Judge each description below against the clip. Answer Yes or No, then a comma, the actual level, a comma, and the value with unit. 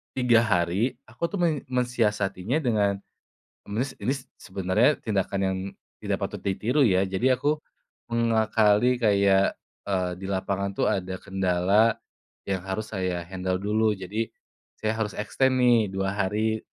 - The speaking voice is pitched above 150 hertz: No, low, 105 Hz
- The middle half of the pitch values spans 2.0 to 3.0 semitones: No, average, 3.5 semitones